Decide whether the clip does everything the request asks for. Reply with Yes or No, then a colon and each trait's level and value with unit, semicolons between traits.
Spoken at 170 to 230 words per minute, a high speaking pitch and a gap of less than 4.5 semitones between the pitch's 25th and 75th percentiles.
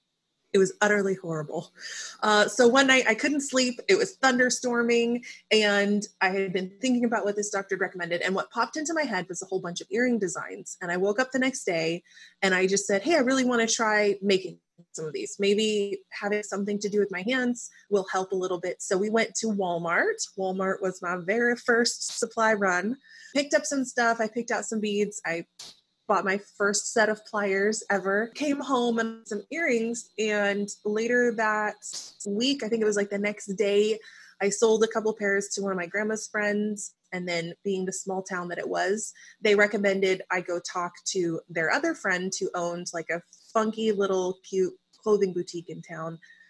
Yes: fast, 205 wpm; high, 205 Hz; average, 3.4 semitones